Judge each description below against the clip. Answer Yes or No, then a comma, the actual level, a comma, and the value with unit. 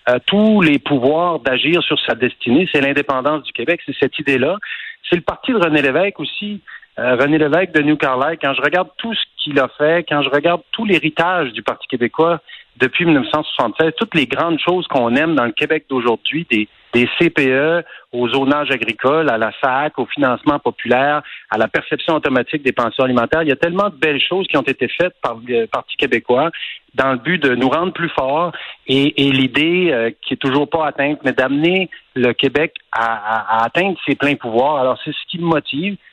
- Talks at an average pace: Yes, average, 205 wpm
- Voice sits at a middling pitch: Yes, medium, 150 Hz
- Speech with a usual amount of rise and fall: Yes, average, 4.4 semitones